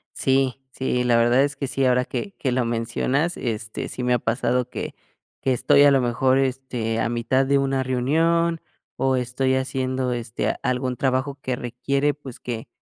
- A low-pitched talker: Yes, low, 130 Hz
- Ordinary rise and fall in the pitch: No, narrow, 1.7 semitones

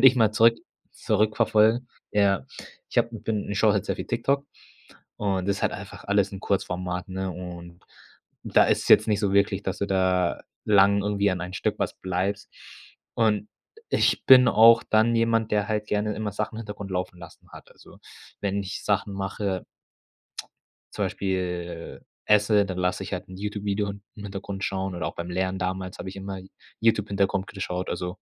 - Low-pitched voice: Yes, low, 100 Hz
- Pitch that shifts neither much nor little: No, narrow, 2.2 semitones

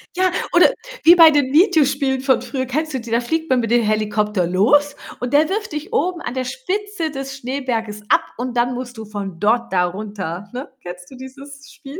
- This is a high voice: Yes, very high, 260 Hz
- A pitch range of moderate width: Yes, average, 5.0 semitones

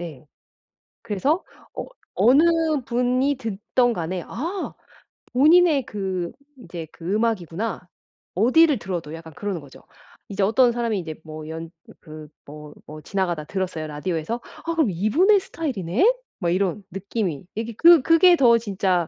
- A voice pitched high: Yes, high, 200 Hz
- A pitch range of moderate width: No, wide, 6.9 semitones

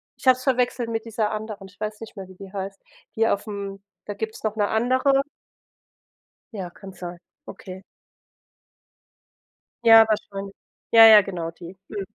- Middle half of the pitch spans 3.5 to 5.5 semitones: No, narrow, 2.5 semitones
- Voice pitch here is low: No, high, 210 Hz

